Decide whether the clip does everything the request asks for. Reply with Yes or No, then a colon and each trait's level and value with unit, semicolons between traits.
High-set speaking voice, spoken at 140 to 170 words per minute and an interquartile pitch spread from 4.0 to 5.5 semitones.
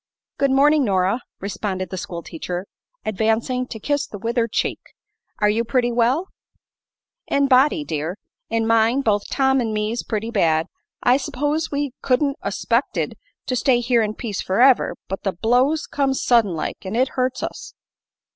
Yes: high, 235 Hz; average, 160 wpm; average, 4.4 semitones